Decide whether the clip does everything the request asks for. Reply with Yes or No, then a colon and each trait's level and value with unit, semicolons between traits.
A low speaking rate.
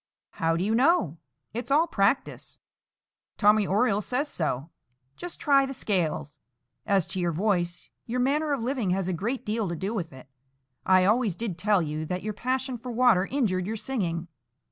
No: average, 180 wpm